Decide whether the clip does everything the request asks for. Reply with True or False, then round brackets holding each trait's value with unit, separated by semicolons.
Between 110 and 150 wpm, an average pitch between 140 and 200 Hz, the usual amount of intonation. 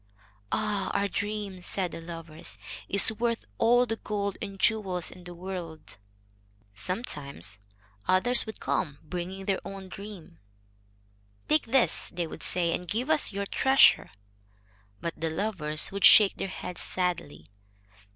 True (140 wpm; 190 Hz; 3.8 semitones)